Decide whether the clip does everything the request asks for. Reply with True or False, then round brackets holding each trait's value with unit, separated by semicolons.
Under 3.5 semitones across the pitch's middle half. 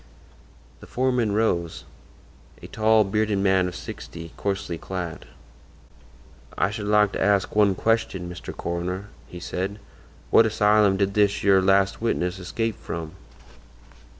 True (2.8 semitones)